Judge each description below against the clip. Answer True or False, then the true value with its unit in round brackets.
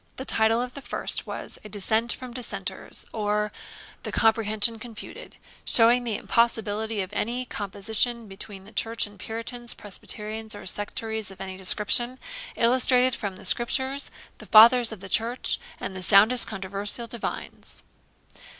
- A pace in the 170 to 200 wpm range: False (145 wpm)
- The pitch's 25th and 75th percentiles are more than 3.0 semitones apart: False (2.6 semitones)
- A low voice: False (220 Hz)